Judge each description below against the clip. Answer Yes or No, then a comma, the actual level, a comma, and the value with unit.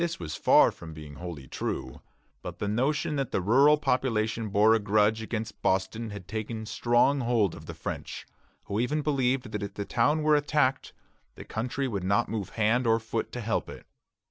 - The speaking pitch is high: No, low, 110 Hz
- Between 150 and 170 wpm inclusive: No, average, 195 wpm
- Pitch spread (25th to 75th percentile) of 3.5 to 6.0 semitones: Yes, average, 4.0 semitones